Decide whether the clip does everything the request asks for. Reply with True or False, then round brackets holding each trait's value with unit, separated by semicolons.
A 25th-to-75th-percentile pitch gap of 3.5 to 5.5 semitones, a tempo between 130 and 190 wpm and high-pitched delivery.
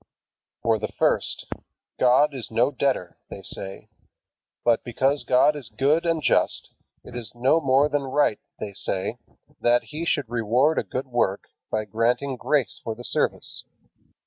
False (3.9 semitones; 155 wpm; 125 Hz)